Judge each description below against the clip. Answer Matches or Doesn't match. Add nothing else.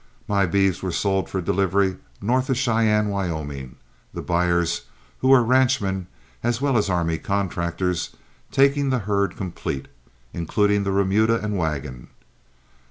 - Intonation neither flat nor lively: Matches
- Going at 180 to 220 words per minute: Doesn't match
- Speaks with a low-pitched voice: Matches